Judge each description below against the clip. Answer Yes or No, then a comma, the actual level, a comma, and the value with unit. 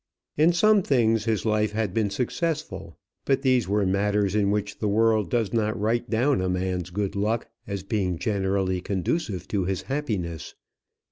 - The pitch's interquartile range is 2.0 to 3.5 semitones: Yes, average, 3.2 semitones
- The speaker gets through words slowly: No, average, 165 wpm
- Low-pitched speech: Yes, low, 105 Hz